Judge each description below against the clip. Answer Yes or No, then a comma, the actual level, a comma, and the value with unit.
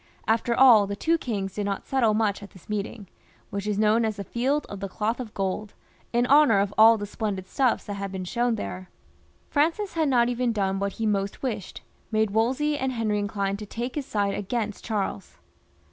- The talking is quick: Yes, fast, 210 wpm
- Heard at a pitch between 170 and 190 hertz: No, high, 215 Hz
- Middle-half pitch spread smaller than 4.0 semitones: Yes, average, 3.3 semitones